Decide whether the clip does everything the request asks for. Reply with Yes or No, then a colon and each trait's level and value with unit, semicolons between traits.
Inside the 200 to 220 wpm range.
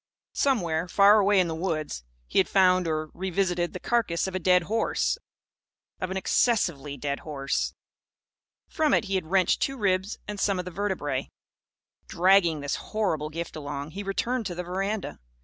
No: average, 170 wpm